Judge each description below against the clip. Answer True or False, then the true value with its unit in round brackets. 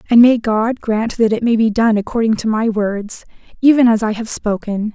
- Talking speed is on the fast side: True (220 wpm)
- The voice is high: True (220 Hz)